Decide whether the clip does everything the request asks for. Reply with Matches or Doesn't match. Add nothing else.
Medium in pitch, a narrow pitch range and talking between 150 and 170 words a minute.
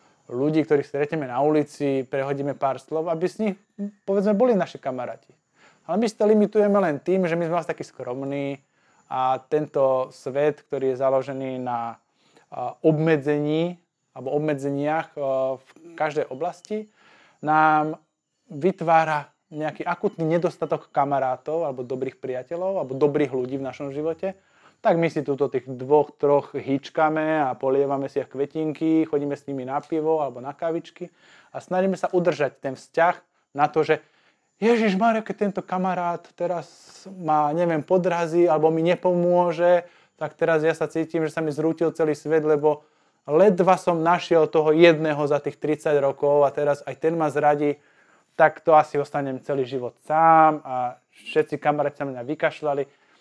Doesn't match